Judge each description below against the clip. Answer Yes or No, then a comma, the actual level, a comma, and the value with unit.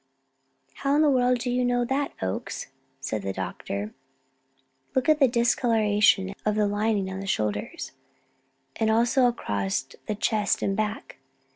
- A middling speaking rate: Yes, average, 150 wpm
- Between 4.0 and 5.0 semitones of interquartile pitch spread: Yes, average, 4.4 semitones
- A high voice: Yes, high, 215 Hz